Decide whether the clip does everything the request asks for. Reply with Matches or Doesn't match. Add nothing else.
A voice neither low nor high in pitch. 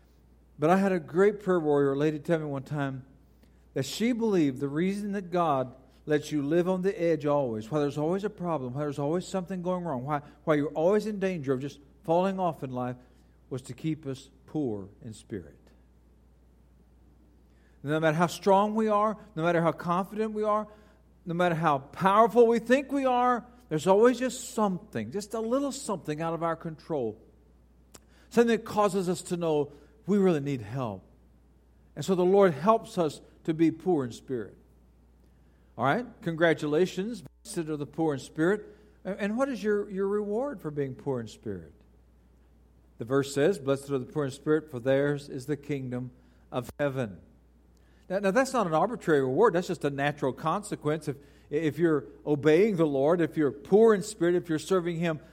Matches